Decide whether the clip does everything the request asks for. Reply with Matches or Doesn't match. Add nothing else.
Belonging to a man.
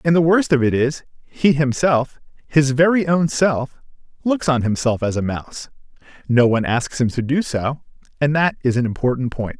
Matches